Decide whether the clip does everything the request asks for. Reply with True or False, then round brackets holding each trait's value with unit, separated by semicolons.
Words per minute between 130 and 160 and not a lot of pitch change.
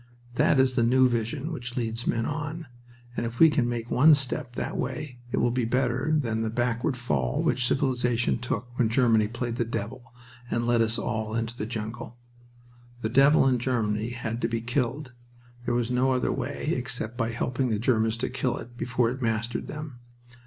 False (195 wpm; 2.1 semitones)